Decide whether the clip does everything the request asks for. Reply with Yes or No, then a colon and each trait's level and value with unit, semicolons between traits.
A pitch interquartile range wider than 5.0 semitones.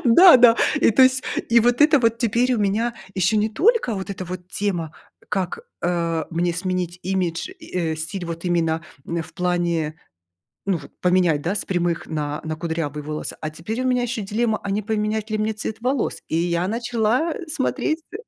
Yes: wide, 5.4 semitones